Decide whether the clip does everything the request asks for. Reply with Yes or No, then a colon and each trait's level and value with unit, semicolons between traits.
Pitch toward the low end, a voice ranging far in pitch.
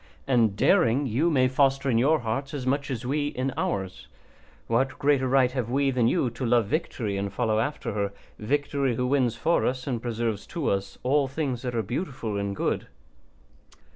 No: low, 125 Hz; average, 3.4 semitones